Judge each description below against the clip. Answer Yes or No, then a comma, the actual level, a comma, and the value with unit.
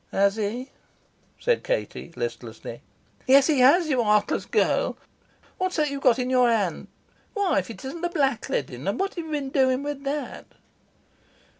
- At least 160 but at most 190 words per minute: Yes, average, 170 wpm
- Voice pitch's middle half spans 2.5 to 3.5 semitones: No, average, 5.1 semitones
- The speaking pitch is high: Yes, very high, 270 Hz